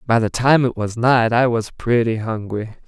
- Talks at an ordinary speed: No, fast, 210 wpm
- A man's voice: Yes, male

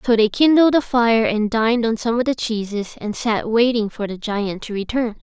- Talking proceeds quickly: Yes, fast, 225 wpm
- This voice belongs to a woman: Yes, female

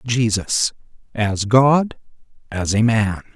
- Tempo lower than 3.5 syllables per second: Yes, 3.1 syllables/s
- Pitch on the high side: No, low, 115 Hz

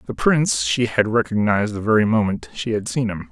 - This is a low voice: Yes, low, 110 Hz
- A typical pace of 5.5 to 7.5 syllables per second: Yes, 5.8 syllables/s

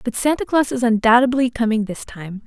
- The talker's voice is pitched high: Yes, high, 235 Hz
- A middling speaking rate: Yes, average, 195 wpm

